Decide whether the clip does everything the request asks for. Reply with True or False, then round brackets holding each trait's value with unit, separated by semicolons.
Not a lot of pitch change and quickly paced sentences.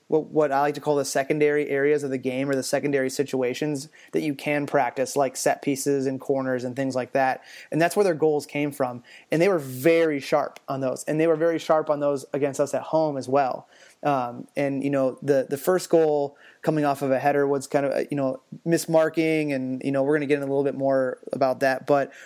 True (1.8 semitones; 240 wpm)